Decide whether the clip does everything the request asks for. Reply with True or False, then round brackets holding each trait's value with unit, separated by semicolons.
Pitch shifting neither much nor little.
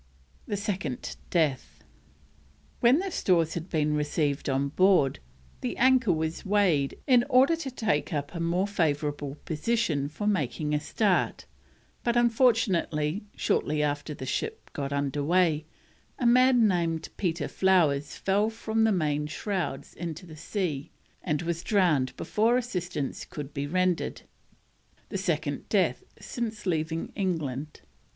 False (5.8 semitones)